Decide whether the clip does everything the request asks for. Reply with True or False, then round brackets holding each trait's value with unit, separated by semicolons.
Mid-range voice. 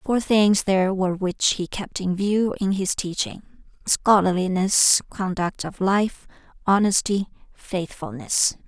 False (195 Hz)